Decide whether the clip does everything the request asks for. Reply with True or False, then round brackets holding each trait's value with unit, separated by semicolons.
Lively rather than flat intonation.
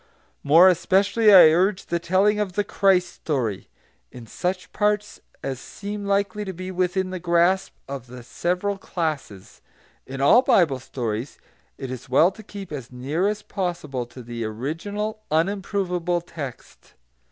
True (6.4 semitones)